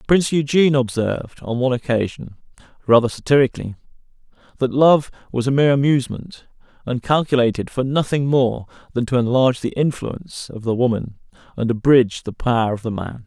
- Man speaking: Yes, male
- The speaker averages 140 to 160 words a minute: Yes, average, 155 wpm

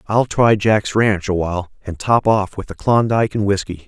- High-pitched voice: No, low, 105 Hz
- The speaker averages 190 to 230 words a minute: Yes, average, 200 wpm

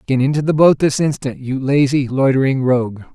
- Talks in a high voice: No, low, 135 Hz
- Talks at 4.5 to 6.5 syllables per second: Yes, 5.5 syllables/s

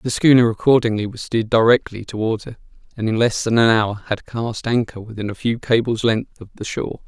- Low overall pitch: Yes, low, 115 Hz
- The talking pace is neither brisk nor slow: No, fast, 210 wpm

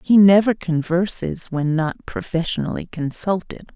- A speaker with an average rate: No, slow, 110 wpm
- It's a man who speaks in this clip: No, female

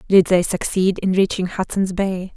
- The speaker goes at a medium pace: Yes, average, 180 wpm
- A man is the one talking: No, female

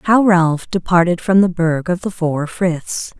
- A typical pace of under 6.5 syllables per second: Yes, 3.9 syllables/s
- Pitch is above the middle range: No, medium, 175 Hz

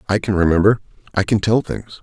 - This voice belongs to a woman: No, male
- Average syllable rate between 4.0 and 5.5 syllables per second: No, 6.1 syllables/s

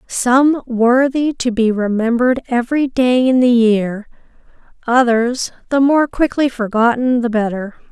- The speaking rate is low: Yes, slow, 130 wpm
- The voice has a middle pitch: No, high, 245 Hz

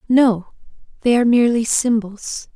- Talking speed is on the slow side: Yes, slow, 120 wpm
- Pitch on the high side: Yes, high, 230 Hz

